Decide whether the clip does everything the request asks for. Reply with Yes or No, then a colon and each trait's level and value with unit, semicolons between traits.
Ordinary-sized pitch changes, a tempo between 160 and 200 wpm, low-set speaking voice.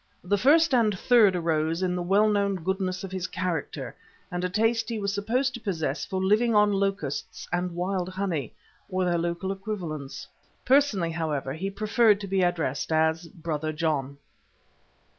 No: average, 3.8 semitones; average, 165 wpm; medium, 185 Hz